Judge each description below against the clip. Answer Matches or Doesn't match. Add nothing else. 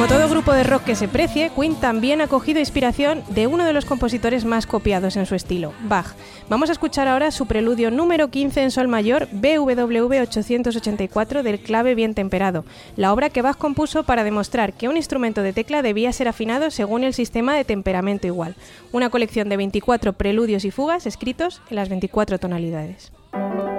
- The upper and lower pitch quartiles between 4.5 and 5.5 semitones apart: Matches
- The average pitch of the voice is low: Doesn't match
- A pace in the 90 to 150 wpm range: Doesn't match